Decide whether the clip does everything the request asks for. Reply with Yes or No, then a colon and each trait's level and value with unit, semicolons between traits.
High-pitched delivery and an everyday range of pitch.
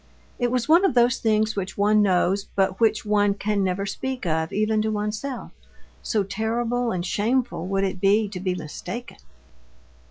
Yes: high, 210 Hz; average, 3.2 semitones